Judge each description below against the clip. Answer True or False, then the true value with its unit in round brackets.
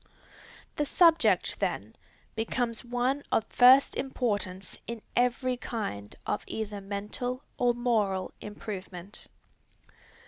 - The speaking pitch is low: False (230 Hz)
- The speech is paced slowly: True (100 wpm)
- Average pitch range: True (3.6 semitones)